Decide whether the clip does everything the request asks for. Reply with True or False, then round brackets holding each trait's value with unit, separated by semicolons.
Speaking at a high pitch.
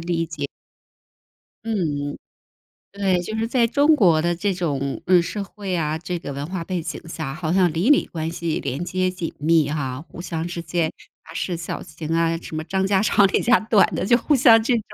False (175 Hz)